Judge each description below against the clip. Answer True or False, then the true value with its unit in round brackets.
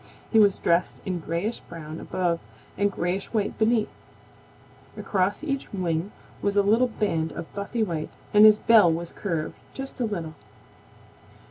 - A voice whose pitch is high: True (200 Hz)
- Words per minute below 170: True (150 wpm)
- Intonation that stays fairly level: False (4.2 semitones)